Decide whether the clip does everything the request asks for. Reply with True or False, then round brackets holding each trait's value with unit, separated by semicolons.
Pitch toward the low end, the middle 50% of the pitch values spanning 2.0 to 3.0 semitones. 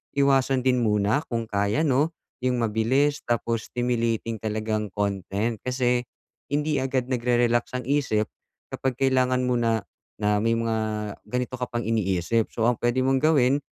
True (120 Hz; 2.6 semitones)